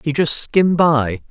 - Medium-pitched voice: Yes, medium, 150 Hz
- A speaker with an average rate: Yes, average, 185 wpm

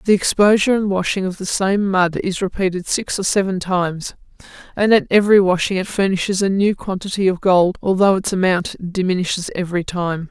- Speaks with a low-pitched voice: No, high, 190 Hz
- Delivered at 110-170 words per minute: No, average, 180 wpm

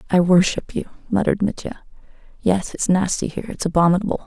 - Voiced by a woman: Yes, female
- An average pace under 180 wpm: Yes, average, 155 wpm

